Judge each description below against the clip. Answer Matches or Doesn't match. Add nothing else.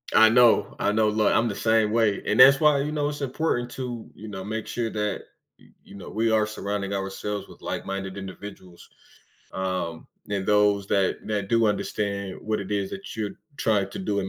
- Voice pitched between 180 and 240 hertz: Doesn't match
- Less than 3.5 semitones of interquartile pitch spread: Matches